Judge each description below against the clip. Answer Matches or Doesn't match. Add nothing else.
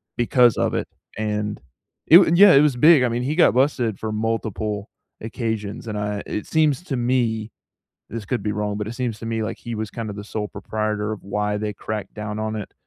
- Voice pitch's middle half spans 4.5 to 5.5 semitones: Doesn't match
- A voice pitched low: Matches